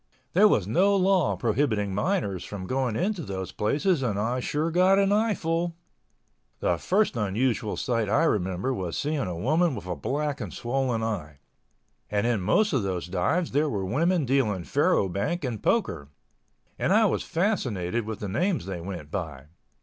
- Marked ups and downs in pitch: Yes, wide, 9.0 semitones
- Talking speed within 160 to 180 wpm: Yes, average, 170 wpm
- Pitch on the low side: Yes, low, 120 Hz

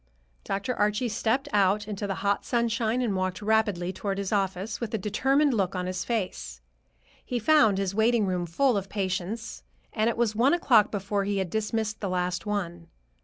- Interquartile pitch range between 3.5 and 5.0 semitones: No, average, 3.0 semitones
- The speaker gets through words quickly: No, average, 185 wpm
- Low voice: No, high, 205 Hz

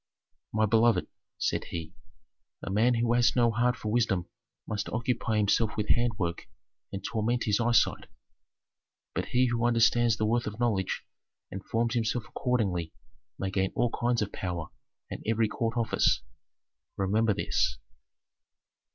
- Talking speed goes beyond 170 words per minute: No, average, 140 wpm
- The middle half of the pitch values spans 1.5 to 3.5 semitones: Yes, narrow, 2.6 semitones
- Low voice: Yes, low, 115 Hz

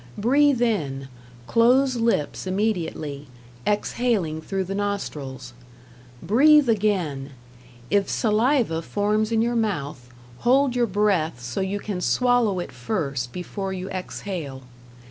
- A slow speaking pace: Yes, slow, 115 wpm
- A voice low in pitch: No, high, 200 Hz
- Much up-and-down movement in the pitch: Yes, wide, 6.5 semitones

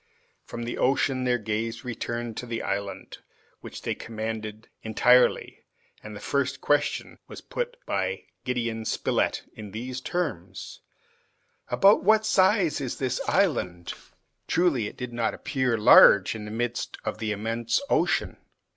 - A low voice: Yes, low, 120 Hz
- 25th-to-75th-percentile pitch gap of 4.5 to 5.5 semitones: No, average, 3.7 semitones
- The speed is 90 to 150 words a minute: Yes, average, 140 wpm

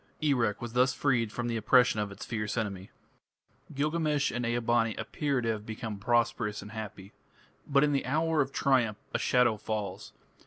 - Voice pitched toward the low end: Yes, low, 120 Hz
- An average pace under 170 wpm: No, average, 180 wpm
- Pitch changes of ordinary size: Yes, average, 4.0 semitones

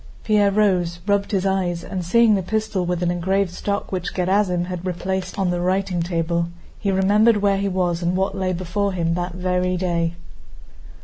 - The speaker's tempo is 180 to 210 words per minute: Yes, average, 185 wpm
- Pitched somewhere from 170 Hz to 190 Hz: Yes, medium, 185 Hz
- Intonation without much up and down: Yes, narrow, 2.1 semitones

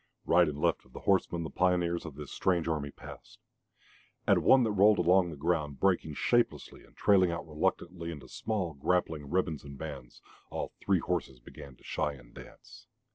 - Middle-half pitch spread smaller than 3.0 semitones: No, average, 4.0 semitones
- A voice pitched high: No, very low, 85 Hz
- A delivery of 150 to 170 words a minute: No, average, 185 wpm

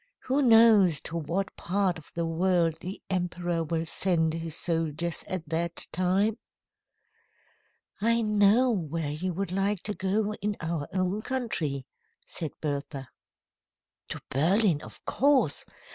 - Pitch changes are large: No, average, 3.9 semitones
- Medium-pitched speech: Yes, medium, 180 Hz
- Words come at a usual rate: No, slow, 130 wpm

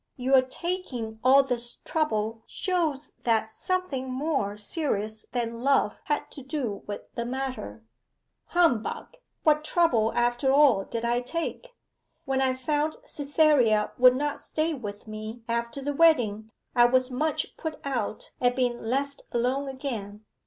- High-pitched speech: Yes, very high, 255 Hz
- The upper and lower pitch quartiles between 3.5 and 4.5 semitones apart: Yes, average, 4.1 semitones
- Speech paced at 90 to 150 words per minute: Yes, average, 140 wpm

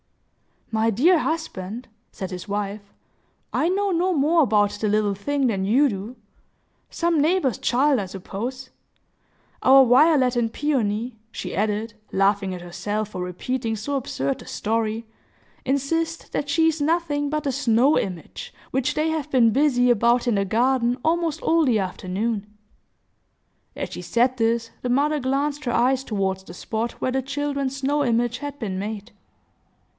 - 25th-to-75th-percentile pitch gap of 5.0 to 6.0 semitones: Yes, wide, 5.4 semitones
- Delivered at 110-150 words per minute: No, average, 160 wpm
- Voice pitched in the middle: No, high, 245 Hz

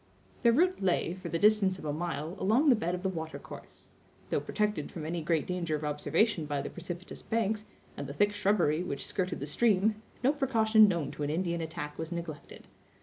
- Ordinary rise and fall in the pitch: Yes, average, 5.0 semitones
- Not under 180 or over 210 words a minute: Yes, fast, 205 wpm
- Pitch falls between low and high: Yes, medium, 180 Hz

